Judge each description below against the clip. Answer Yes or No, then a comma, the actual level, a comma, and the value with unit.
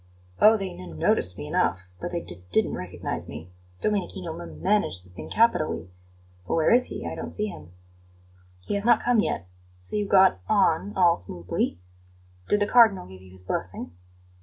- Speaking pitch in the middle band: Yes, medium, 175 Hz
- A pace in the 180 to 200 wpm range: Yes, average, 185 wpm